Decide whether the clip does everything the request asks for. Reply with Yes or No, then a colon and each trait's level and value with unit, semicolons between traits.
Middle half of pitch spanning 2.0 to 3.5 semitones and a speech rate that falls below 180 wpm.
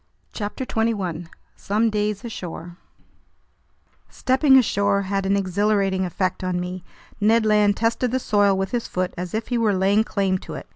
Yes: average, 2.9 semitones; average, 160 wpm